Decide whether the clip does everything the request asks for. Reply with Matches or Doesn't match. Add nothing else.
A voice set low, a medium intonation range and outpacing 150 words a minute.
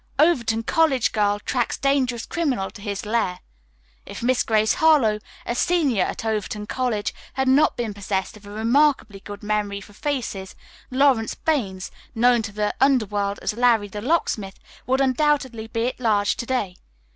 Doesn't match